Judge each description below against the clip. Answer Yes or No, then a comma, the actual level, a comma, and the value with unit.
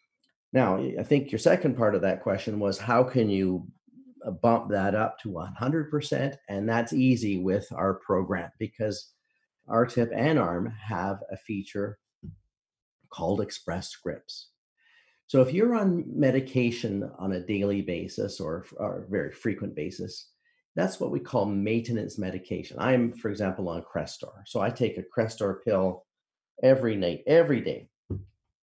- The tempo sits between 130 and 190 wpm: Yes, average, 145 wpm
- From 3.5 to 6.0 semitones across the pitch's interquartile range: Yes, average, 4.5 semitones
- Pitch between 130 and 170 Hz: No, low, 110 Hz